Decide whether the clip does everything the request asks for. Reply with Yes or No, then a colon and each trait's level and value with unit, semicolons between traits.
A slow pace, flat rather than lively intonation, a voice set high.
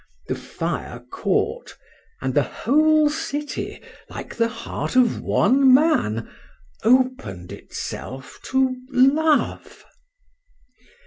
No: slow, 85 wpm; average, 4.5 semitones; very high, 260 Hz